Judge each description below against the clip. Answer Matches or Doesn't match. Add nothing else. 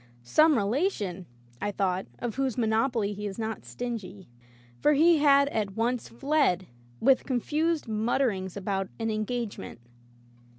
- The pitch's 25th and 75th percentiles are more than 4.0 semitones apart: Matches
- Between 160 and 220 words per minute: Doesn't match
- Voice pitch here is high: Matches